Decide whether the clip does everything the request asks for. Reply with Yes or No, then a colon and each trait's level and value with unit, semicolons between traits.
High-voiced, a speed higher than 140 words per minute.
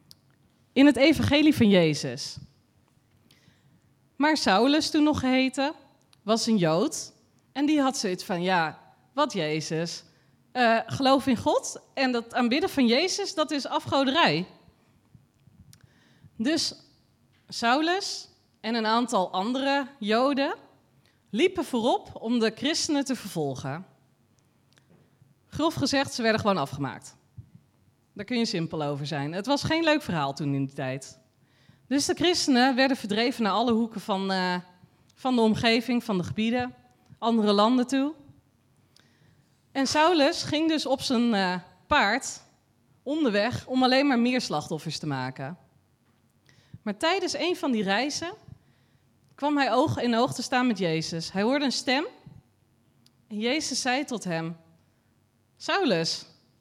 No: high, 220 Hz; slow, 135 wpm